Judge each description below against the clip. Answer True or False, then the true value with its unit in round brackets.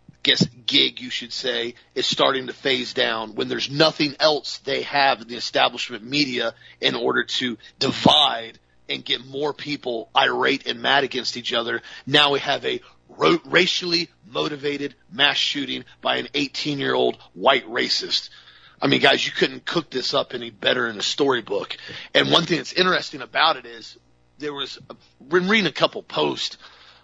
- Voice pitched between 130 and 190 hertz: True (140 Hz)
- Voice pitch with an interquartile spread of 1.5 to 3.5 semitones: False (4.2 semitones)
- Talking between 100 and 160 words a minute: False (175 wpm)